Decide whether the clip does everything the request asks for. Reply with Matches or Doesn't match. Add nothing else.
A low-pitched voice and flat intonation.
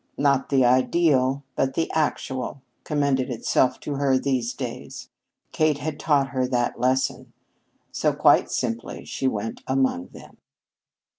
Matches